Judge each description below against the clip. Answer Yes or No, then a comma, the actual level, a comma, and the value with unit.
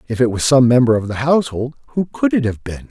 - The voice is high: No, low, 125 Hz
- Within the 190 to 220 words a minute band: No, fast, 270 wpm